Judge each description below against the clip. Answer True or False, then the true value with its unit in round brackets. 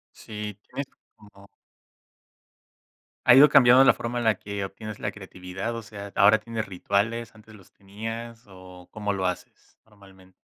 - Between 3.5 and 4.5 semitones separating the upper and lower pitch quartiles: False (2.7 semitones)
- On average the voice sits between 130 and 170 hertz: False (105 Hz)